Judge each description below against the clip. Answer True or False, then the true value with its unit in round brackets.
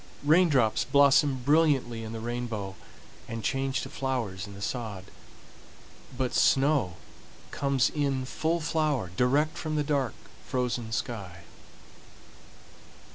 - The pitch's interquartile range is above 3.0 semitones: True (4.2 semitones)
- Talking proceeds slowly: True (115 wpm)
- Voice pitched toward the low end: True (130 Hz)